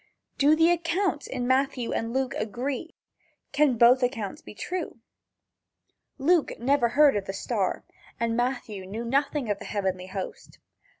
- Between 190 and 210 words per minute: No, average, 145 wpm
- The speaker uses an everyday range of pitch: Yes, average, 4.6 semitones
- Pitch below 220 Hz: No, very high, 250 Hz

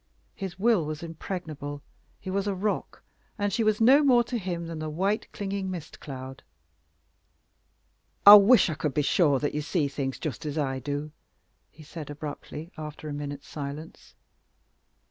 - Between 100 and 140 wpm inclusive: No, average, 165 wpm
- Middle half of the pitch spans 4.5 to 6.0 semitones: Yes, average, 5.3 semitones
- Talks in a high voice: No, medium, 160 Hz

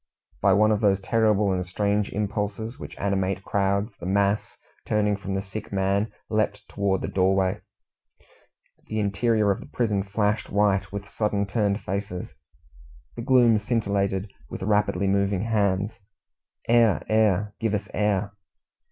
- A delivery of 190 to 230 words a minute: No, average, 145 wpm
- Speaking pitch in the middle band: No, low, 100 Hz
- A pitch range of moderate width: No, narrow, 1.6 semitones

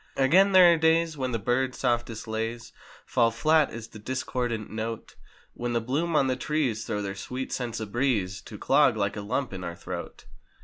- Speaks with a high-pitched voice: No, low, 120 Hz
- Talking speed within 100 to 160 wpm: No, average, 195 wpm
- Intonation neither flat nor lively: Yes, average, 3.5 semitones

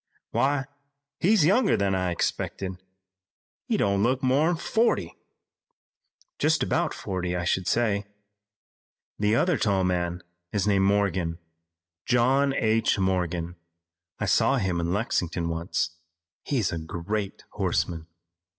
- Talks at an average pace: No, slow, 120 wpm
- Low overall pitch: Yes, low, 100 Hz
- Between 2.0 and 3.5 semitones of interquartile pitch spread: No, average, 5.3 semitones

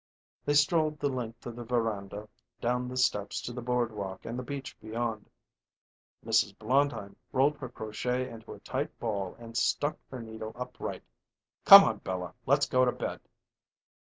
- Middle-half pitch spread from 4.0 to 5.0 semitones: No, average, 2.8 semitones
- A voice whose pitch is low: Yes, low, 120 Hz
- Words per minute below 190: Yes, average, 160 wpm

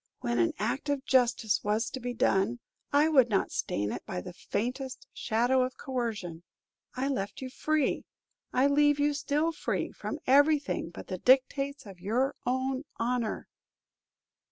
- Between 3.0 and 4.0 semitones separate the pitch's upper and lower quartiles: No, average, 4.6 semitones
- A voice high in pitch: Yes, very high, 255 Hz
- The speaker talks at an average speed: Yes, average, 155 wpm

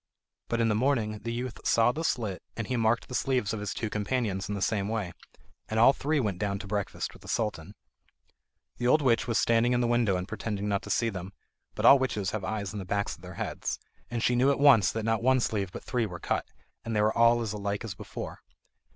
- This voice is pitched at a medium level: No, low, 110 Hz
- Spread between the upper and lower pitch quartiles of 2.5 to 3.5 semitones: Yes, average, 2.9 semitones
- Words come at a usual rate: No, fast, 245 wpm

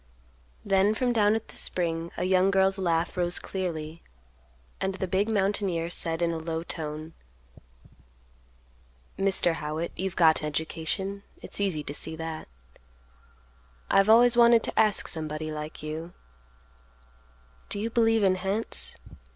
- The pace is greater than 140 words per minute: No, slow, 135 wpm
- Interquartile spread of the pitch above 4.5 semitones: No, average, 3.7 semitones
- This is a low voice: No, medium, 180 Hz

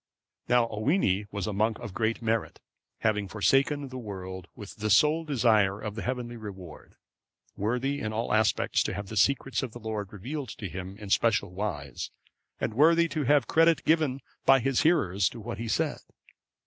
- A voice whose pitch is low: Yes, low, 110 Hz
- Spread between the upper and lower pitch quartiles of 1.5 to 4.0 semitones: No, average, 4.8 semitones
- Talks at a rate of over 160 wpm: Yes, average, 180 wpm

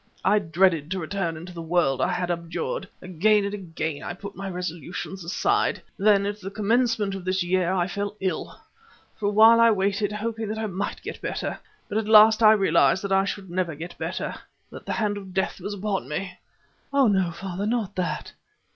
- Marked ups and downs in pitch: No, average, 2.9 semitones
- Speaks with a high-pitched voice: Yes, high, 195 Hz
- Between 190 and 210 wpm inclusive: Yes, average, 200 wpm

